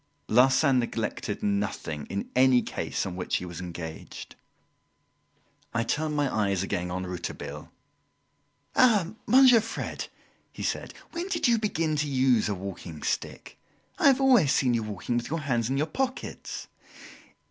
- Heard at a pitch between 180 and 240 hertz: No, low, 125 Hz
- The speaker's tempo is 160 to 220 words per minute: No, average, 150 wpm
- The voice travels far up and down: Yes, wide, 8.7 semitones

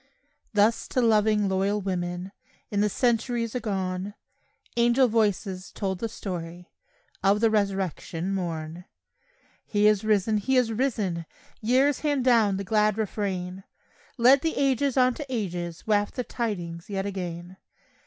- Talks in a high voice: Yes, high, 205 Hz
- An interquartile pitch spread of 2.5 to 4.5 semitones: Yes, average, 3.8 semitones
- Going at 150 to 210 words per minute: No, slow, 135 wpm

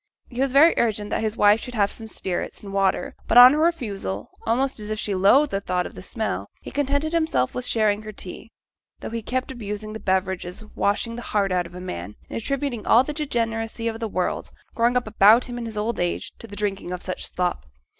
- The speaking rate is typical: No, fast, 235 wpm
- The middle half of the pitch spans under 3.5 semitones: No, average, 3.8 semitones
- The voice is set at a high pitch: Yes, high, 220 Hz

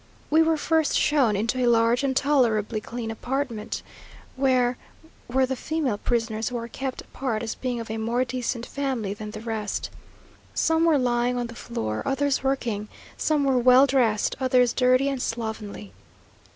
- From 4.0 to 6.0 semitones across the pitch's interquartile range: No, average, 3.1 semitones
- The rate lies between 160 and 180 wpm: Yes, average, 165 wpm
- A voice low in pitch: No, high, 245 Hz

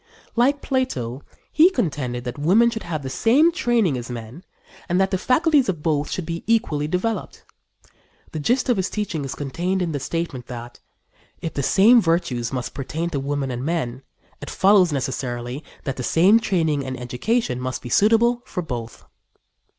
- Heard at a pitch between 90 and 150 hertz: No, medium, 160 Hz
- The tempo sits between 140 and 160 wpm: No, average, 175 wpm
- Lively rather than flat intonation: Yes, wide, 8.5 semitones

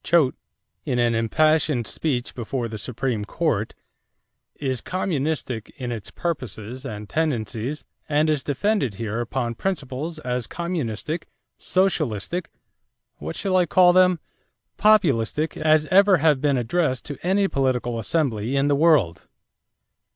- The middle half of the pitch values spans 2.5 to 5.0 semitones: No, wide, 5.5 semitones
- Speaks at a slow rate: Yes, slow, 130 wpm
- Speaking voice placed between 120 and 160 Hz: Yes, medium, 140 Hz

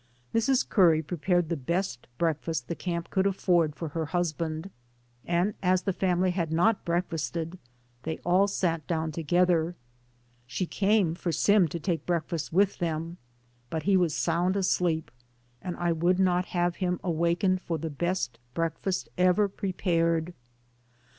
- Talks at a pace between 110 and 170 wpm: Yes, average, 155 wpm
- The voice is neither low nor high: Yes, medium, 175 Hz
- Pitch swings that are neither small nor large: No, narrow, 2.2 semitones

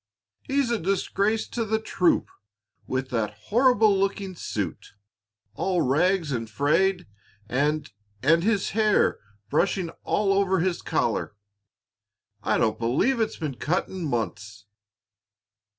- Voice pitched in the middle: Yes, medium, 180 Hz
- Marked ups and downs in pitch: Yes, wide, 7.2 semitones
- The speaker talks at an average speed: No, slow, 120 wpm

